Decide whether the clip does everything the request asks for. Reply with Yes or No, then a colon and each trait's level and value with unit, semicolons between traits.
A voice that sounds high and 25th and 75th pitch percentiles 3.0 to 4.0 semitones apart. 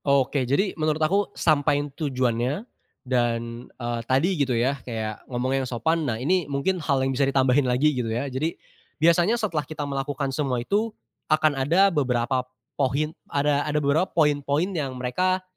No: medium, 140 Hz; average, 3.4 semitones